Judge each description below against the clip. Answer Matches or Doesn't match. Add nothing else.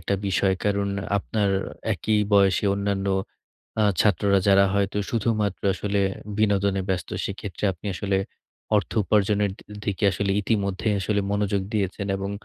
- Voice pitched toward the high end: Doesn't match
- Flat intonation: Matches